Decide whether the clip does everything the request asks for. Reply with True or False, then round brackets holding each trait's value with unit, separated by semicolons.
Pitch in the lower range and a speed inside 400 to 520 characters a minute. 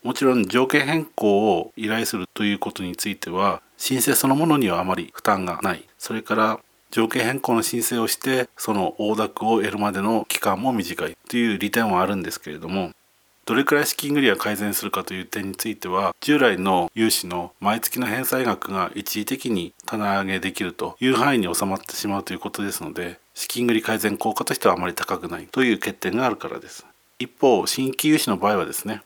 True (110 Hz; 410 characters per minute)